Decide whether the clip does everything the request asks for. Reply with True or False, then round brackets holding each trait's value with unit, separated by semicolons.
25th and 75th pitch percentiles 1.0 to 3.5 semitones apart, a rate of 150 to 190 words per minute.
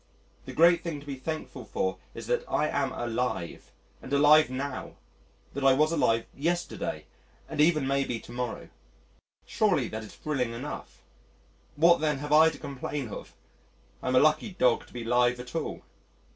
False (3.9 semitones; 170 wpm)